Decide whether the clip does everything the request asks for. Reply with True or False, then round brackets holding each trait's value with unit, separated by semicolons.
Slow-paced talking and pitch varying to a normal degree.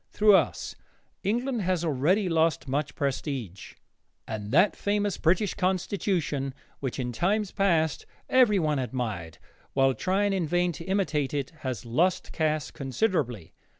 False (130 wpm; 6.3 semitones)